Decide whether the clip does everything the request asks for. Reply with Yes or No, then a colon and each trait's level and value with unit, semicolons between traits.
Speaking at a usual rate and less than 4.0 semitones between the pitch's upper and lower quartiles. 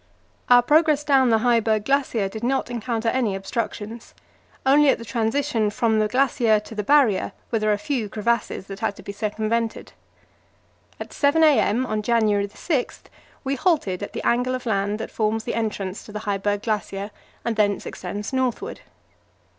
Yes: average, 170 wpm; average, 3.5 semitones